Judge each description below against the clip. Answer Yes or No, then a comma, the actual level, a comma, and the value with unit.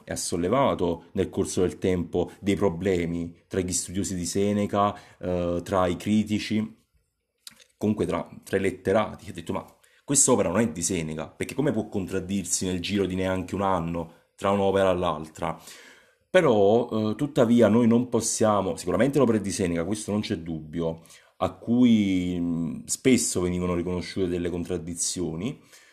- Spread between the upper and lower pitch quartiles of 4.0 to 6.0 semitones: No, average, 3.2 semitones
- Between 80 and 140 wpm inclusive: No, average, 155 wpm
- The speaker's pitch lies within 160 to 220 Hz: No, very low, 95 Hz